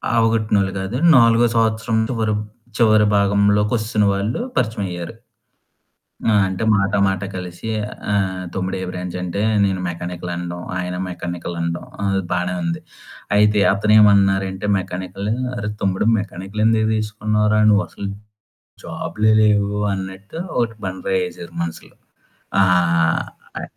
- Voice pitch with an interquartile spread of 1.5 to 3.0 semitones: Yes, narrow, 2.6 semitones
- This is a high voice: No, low, 100 Hz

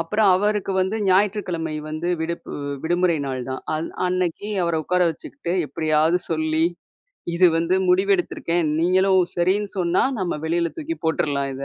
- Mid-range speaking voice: Yes, medium, 175 Hz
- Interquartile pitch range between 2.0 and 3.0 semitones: Yes, average, 2.7 semitones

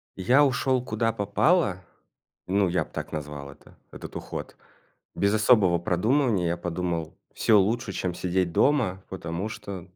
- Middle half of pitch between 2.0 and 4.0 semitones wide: No, average, 4.6 semitones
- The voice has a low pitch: Yes, very low, 95 Hz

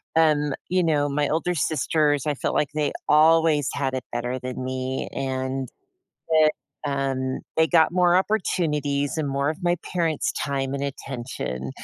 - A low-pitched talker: No, medium, 145 Hz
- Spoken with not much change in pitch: No, average, 3.2 semitones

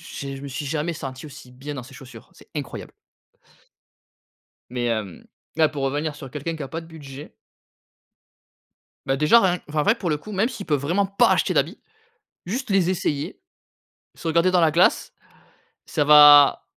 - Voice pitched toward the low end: No, medium, 150 Hz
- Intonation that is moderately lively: Yes, average, 3.8 semitones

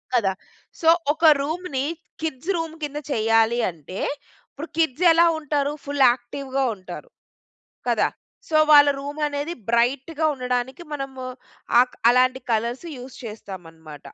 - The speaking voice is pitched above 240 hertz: Yes, very high, 265 Hz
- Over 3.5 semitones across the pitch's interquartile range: Yes, average, 4.0 semitones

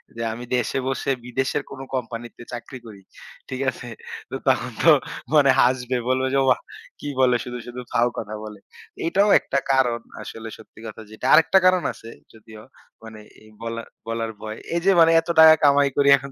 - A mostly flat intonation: No, average, 3.3 semitones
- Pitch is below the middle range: Yes, low, 125 Hz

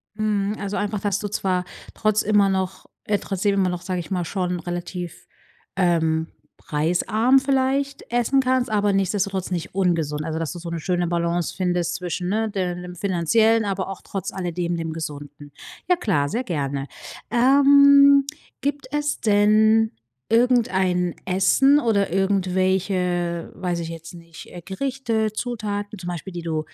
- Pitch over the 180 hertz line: Yes, high, 190 Hz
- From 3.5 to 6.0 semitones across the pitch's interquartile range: Yes, average, 3.8 semitones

